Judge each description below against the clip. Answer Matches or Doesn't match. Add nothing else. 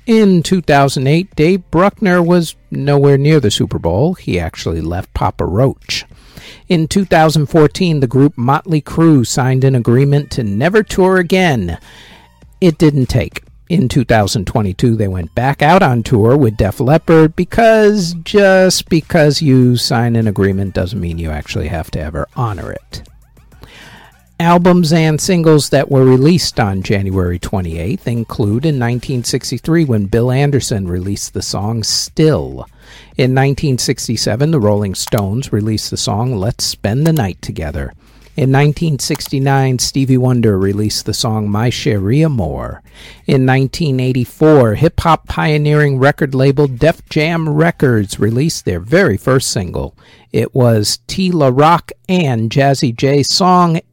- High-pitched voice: Doesn't match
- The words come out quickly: Doesn't match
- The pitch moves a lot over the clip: Matches